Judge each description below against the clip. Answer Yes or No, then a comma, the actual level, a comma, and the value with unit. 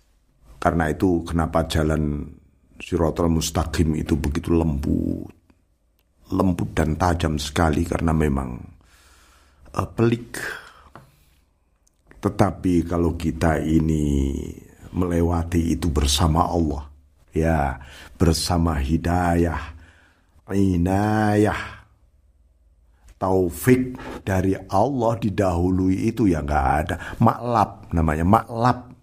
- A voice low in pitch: Yes, very low, 85 Hz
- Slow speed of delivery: Yes, slow, 80 wpm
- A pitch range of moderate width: Yes, average, 3.4 semitones